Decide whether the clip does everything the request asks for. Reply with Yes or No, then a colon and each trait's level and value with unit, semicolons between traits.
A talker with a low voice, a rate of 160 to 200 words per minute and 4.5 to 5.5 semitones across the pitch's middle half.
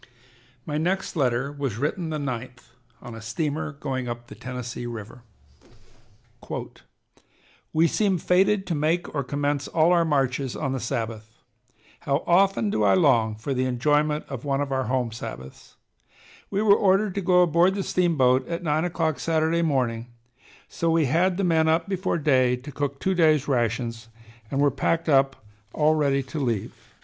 No: medium, 145 Hz; average, 170 wpm; average, 4.8 semitones